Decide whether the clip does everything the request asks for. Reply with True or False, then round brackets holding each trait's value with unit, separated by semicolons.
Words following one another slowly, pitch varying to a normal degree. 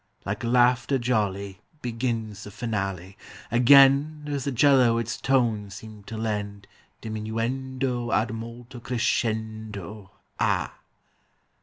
True (105 wpm; 3.0 semitones)